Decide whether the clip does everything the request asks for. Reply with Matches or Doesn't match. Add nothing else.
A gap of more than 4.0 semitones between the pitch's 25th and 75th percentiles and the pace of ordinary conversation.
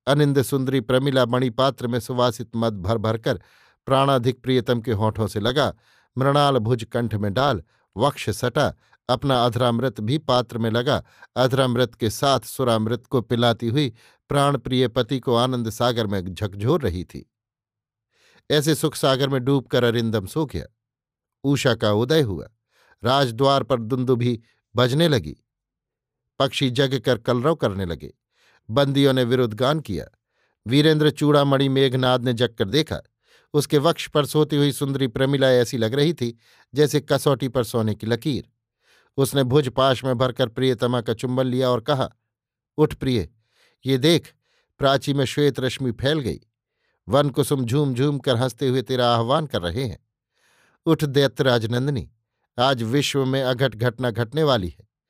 Doesn't match